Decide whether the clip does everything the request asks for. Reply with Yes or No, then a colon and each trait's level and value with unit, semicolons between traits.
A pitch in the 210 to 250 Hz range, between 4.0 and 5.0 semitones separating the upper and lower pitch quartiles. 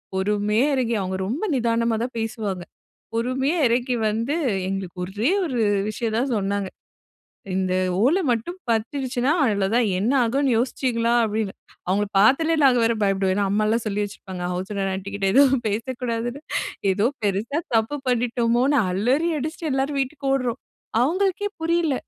Yes: high, 230 Hz; average, 4.6 semitones